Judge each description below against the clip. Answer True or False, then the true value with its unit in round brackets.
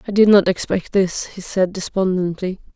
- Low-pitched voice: False (185 Hz)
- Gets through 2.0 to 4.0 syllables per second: False (4.9 syllables/s)